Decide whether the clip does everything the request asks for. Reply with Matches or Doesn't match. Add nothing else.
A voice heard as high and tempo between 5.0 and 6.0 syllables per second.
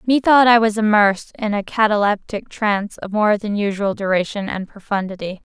Matches